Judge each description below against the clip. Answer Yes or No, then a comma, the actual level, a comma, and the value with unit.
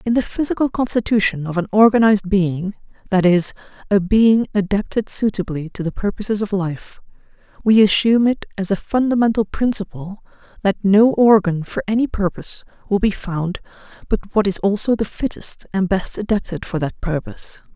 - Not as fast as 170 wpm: Yes, average, 160 wpm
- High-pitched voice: Yes, high, 205 Hz